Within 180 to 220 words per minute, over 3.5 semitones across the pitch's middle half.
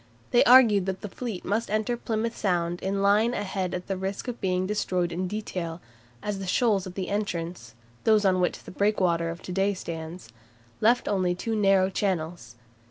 No: average, 185 wpm; average, 2.8 semitones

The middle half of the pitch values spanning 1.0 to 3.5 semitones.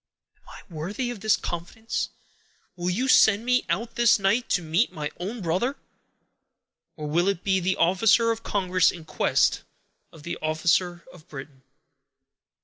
No: average, 5.0 semitones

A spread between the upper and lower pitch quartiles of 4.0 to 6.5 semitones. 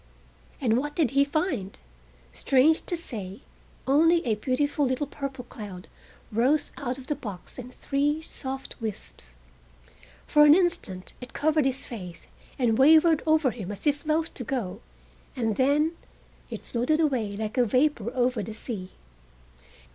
Yes: average, 5.1 semitones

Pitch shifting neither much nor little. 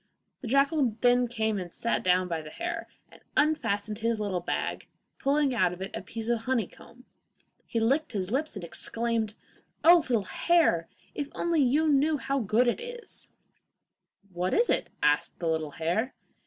No: wide, 6.5 semitones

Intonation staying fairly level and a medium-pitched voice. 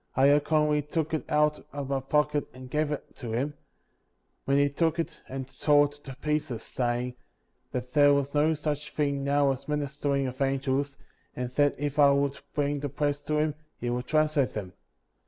Yes: narrow, 1.9 semitones; medium, 145 Hz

